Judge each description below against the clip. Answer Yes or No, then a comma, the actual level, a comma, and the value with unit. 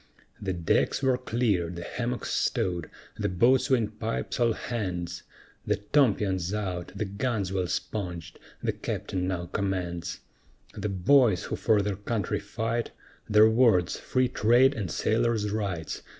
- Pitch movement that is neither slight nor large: Yes, average, 4.5 semitones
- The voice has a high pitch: No, low, 105 Hz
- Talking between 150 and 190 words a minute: No, slow, 135 wpm